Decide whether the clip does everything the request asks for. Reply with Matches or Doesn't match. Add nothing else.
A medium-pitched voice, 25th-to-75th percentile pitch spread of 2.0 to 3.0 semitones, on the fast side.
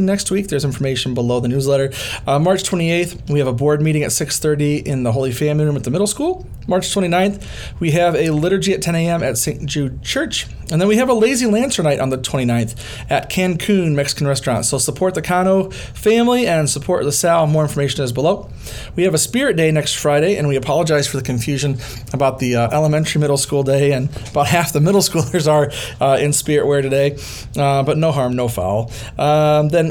Doesn't match